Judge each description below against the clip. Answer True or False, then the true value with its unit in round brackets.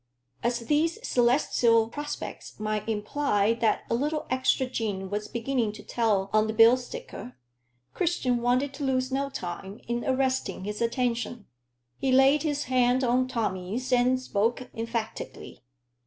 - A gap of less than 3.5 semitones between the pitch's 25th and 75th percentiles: True (2.9 semitones)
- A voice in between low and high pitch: False (245 Hz)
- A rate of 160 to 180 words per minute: False (140 wpm)